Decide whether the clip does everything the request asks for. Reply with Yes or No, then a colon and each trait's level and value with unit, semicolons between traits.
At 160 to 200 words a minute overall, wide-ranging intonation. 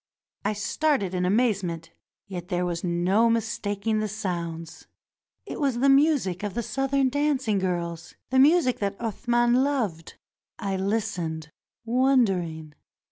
No: slow, 135 wpm; wide, 6.0 semitones